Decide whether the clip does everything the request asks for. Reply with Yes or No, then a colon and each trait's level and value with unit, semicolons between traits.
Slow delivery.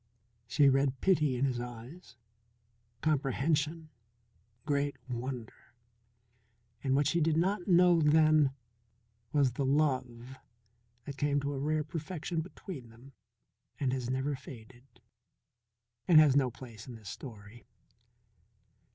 Yes: slow, 120 wpm